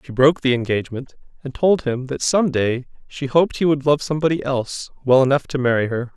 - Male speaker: Yes, male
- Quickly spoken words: Yes, fast, 215 wpm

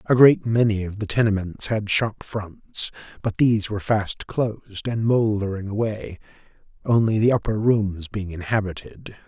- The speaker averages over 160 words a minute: No, average, 150 wpm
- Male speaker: Yes, male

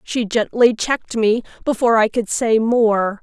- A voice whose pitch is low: No, high, 225 Hz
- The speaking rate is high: No, average, 165 wpm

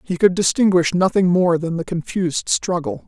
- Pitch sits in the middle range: Yes, medium, 180 Hz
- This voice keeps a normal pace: Yes, average, 175 wpm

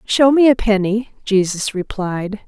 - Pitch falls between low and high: No, high, 210 Hz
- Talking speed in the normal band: Yes, average, 145 wpm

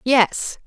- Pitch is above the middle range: Yes, high, 240 Hz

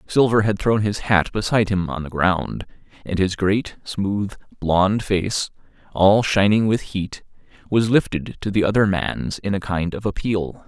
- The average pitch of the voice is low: Yes, low, 100 Hz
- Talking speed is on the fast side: No, average, 175 wpm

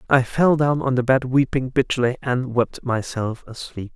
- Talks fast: No, average, 180 wpm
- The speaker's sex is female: No, male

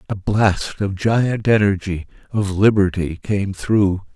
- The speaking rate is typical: No, slow, 130 wpm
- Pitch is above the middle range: No, low, 100 Hz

